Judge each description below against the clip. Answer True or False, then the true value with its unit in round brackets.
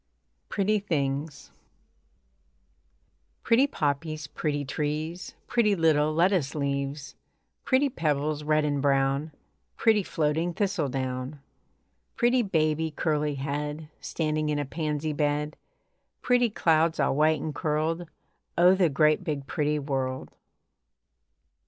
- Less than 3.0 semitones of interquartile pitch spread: True (2.5 semitones)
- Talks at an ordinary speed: False (110 wpm)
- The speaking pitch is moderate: True (155 Hz)